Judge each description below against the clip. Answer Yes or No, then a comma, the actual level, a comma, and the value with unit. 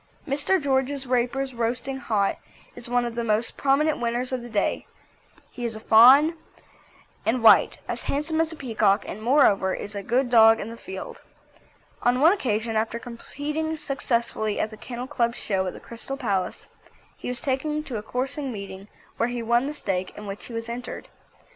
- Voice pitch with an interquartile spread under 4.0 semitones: Yes, average, 3.6 semitones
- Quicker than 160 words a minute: Yes, average, 185 wpm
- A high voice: Yes, high, 240 Hz